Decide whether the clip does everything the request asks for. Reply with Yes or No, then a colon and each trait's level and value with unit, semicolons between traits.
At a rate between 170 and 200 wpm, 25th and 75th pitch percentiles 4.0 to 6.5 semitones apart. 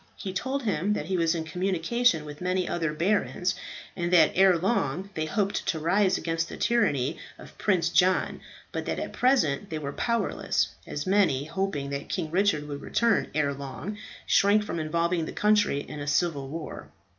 Yes: average, 180 wpm; average, 4.5 semitones